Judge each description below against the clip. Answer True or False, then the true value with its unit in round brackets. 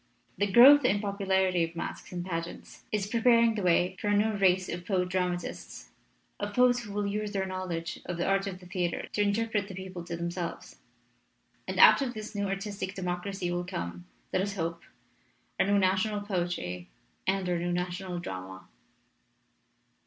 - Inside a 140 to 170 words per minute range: False (180 wpm)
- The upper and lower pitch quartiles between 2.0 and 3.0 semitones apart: True (2.6 semitones)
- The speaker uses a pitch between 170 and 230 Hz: True (190 Hz)